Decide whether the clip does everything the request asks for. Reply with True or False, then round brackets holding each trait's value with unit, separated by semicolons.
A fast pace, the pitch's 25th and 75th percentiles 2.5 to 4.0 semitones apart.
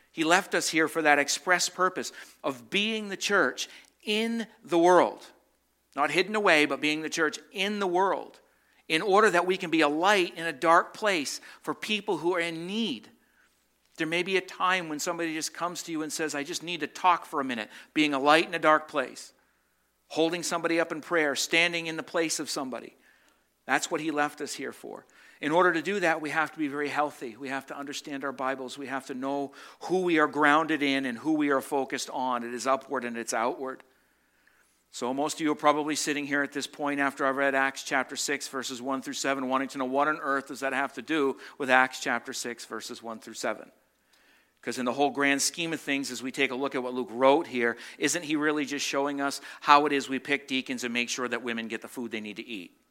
True (235 wpm; 3.7 semitones)